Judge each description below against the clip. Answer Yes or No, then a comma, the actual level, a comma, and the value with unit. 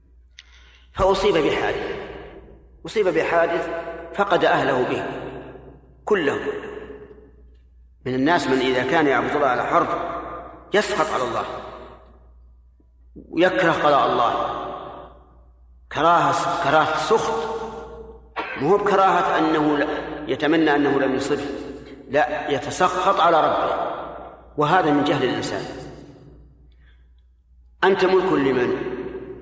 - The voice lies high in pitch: No, medium, 150 Hz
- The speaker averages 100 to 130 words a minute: No, average, 90 wpm